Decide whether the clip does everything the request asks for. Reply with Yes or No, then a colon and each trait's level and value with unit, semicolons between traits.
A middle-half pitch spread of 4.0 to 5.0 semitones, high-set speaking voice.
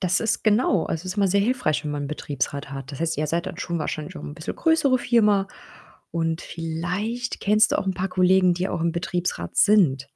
No: average, 4.3 semitones; medium, 180 Hz